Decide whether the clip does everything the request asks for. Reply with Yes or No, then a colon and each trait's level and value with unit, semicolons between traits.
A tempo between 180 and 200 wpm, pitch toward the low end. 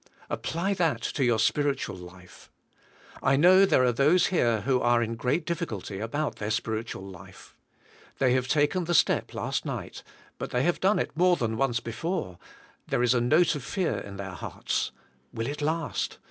Yes: average, 185 wpm; low, 130 Hz